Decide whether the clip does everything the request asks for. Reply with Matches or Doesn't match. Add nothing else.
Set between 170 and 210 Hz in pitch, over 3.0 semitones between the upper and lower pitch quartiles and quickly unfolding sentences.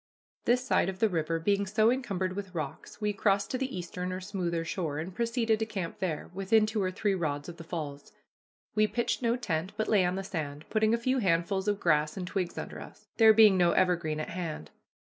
Matches